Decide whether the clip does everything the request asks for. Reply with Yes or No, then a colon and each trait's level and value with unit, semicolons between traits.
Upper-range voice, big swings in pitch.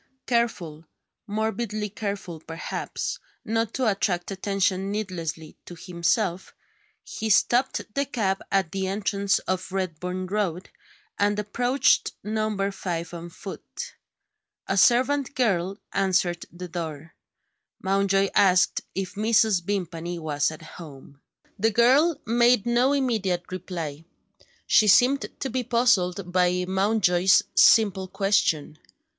No: high, 195 Hz; average, 3.6 semitones